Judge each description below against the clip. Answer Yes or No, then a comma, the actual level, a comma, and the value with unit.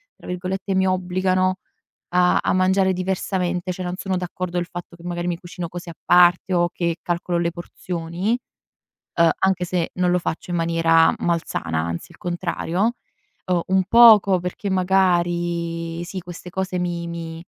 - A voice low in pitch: No, medium, 180 Hz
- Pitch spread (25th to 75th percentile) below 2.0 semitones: Yes, narrow, 1.5 semitones